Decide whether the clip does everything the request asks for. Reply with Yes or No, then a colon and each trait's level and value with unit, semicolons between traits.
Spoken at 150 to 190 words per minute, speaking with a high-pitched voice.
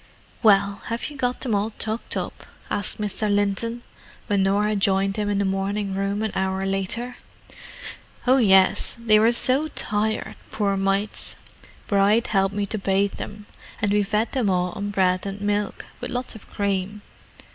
Yes: average, 160 wpm; high, 205 Hz